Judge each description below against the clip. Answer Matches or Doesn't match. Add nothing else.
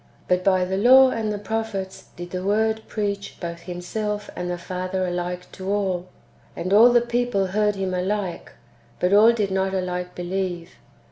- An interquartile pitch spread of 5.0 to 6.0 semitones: Doesn't match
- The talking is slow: Doesn't match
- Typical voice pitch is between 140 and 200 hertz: Matches